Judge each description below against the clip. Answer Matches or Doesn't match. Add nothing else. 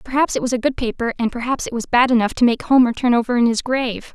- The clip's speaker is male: Doesn't match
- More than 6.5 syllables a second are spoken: Matches